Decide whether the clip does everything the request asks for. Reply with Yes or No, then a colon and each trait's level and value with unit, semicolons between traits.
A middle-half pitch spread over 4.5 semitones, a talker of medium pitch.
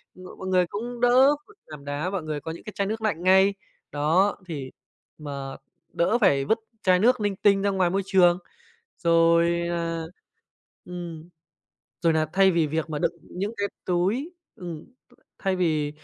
No: average, 3.6 semitones; medium, 180 Hz